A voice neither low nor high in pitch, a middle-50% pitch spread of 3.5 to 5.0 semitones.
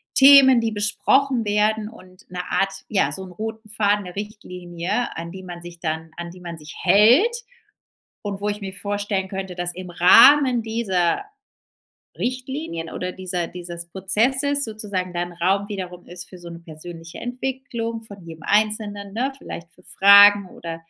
No: high, 195 Hz; average, 3.8 semitones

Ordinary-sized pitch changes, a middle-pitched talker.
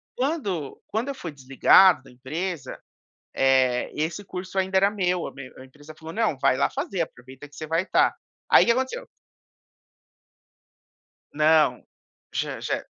No: wide, 5.8 semitones; medium, 160 Hz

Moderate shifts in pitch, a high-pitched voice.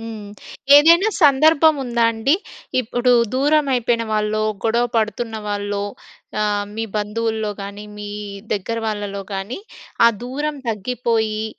Yes: average, 3.1 semitones; high, 225 Hz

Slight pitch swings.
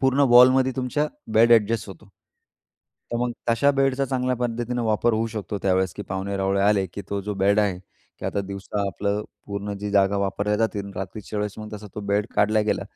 No: average, 3.0 semitones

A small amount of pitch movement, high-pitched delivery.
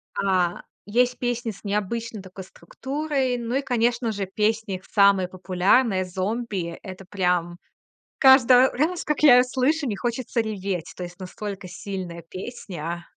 No: average, 4.8 semitones; high, 205 Hz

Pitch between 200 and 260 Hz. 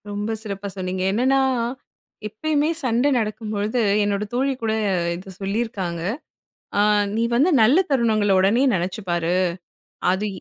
Yes: high, 215 Hz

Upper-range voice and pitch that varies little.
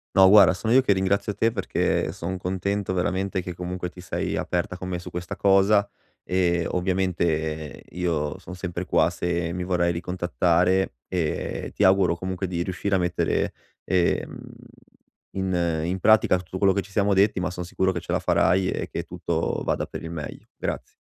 No: very low, 90 Hz; narrow, 1.6 semitones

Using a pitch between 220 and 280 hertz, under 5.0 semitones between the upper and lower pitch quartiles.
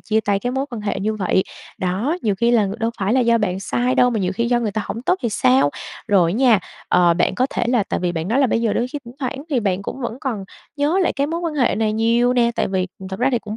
Yes: high, 230 Hz; average, 4.2 semitones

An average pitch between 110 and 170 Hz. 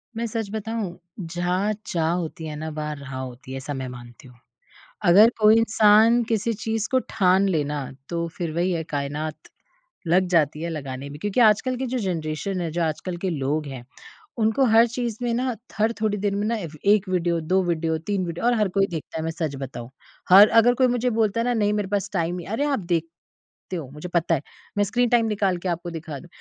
No: medium, 180 Hz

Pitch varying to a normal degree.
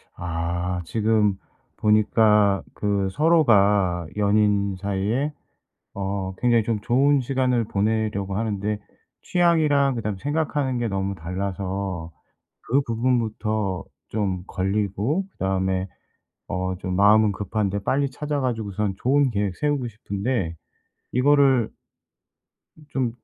Yes: average, 4.4 semitones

